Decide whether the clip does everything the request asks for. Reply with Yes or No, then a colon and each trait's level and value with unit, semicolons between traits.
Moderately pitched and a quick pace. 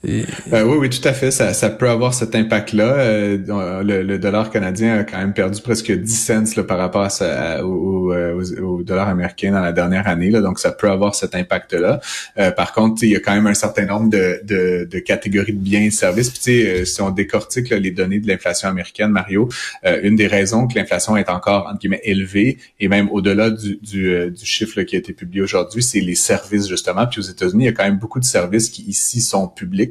No: low, 100 Hz; fast, 235 wpm